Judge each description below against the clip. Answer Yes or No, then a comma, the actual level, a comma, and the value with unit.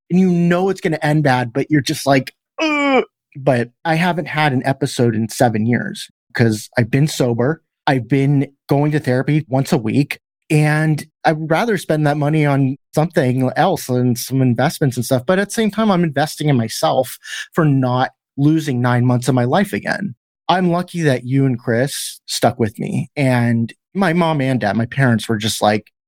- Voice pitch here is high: No, medium, 140 Hz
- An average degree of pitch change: Yes, average, 4.2 semitones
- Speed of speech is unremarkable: Yes, average, 195 wpm